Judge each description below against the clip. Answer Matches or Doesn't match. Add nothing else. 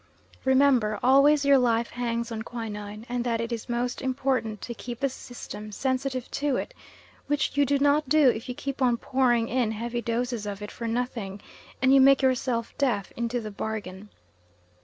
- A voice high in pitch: Matches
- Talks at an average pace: Matches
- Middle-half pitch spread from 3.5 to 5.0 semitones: Doesn't match